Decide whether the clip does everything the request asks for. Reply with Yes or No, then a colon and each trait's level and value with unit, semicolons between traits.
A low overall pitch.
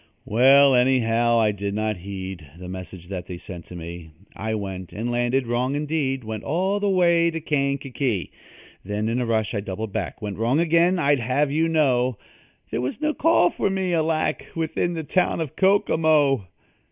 Yes: low, 125 Hz